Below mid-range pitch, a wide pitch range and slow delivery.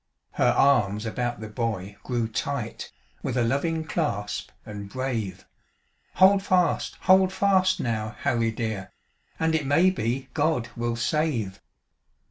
Yes: low, 120 Hz; wide, 6.6 semitones; slow, 130 wpm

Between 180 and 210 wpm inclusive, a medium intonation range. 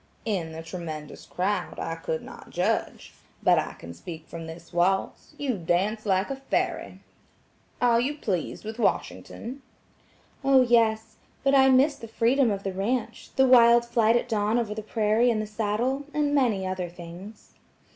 No: average, 165 wpm; average, 4.9 semitones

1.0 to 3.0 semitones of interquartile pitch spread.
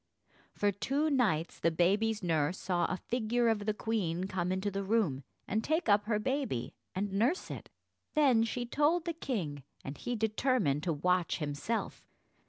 No: wide, 5.6 semitones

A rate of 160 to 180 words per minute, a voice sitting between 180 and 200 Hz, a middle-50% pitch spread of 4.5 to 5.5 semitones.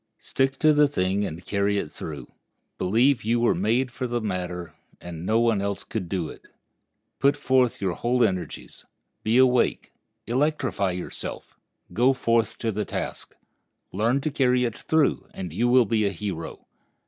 No: average, 170 wpm; low, 115 Hz; average, 4.9 semitones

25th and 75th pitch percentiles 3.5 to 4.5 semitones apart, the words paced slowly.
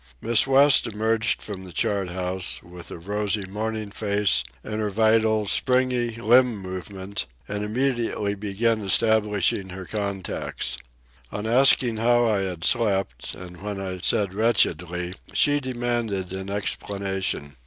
No: average, 3.1 semitones; slow, 130 wpm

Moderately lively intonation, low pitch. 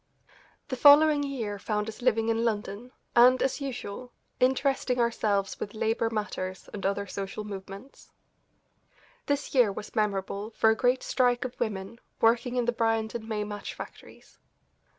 No: average, 3.3 semitones; high, 225 Hz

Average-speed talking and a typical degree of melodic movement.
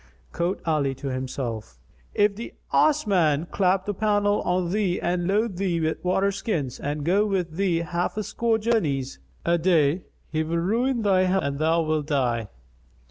Yes: average, 175 wpm; average, 4.6 semitones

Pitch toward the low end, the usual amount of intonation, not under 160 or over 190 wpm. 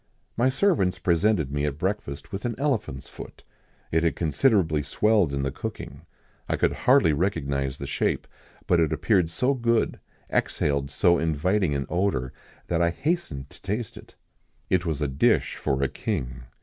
No: very low, 85 Hz; wide, 6.7 semitones; average, 165 wpm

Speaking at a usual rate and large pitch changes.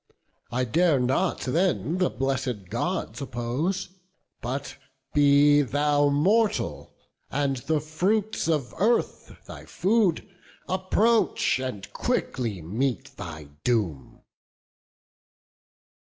No: slow, 95 wpm; wide, 6.5 semitones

